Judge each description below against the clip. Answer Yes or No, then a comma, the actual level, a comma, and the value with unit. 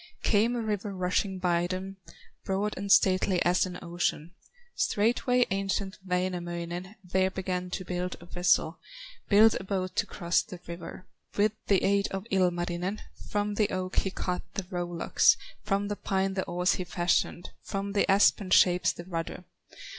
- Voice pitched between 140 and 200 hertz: Yes, medium, 185 Hz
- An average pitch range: No, narrow, 2.0 semitones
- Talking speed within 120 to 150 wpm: No, average, 160 wpm